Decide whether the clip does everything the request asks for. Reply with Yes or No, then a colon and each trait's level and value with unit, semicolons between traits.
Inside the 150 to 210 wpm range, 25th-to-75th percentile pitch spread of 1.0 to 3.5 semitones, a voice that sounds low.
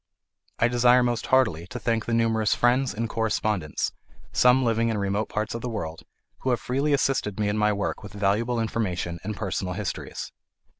Yes: average, 185 wpm; average, 3.0 semitones; low, 110 Hz